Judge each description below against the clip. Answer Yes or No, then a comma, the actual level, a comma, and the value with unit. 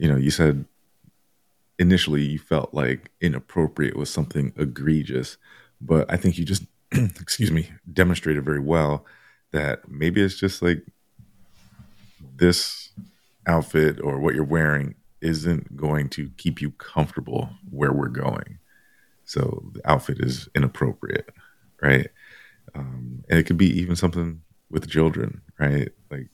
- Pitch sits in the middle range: No, very low, 80 Hz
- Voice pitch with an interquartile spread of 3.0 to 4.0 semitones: Yes, average, 3.5 semitones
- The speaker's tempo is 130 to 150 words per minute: Yes, slow, 135 wpm